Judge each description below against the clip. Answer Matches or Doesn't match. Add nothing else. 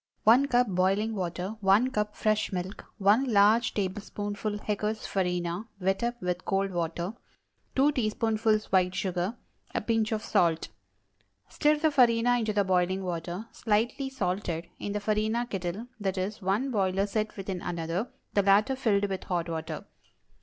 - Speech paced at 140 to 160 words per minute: Matches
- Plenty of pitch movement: Doesn't match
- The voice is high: Matches